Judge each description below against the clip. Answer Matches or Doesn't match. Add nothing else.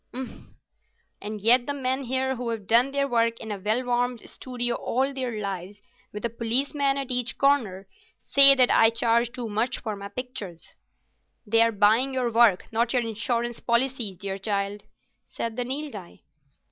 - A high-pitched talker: Matches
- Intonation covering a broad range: Doesn't match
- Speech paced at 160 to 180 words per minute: Matches